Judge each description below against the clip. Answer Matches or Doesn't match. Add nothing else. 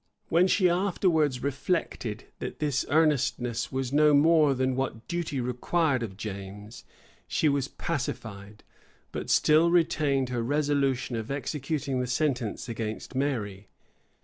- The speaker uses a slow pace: Matches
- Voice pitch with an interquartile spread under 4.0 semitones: Doesn't match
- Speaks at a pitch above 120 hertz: Matches